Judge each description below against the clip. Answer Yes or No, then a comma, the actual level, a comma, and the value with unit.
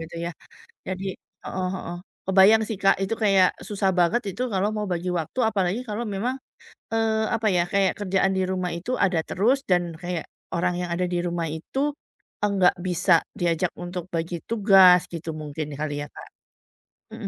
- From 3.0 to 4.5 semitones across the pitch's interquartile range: No, narrow, 2.6 semitones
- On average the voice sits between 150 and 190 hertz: Yes, medium, 185 Hz